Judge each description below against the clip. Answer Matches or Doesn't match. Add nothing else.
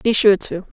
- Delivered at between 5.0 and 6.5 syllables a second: Doesn't match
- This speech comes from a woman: Matches